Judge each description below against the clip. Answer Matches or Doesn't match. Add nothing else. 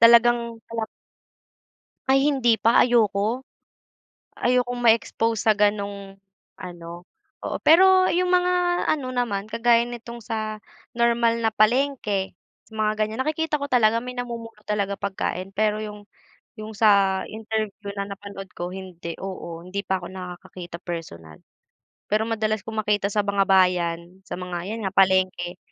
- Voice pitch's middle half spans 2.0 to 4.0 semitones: Matches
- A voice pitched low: Doesn't match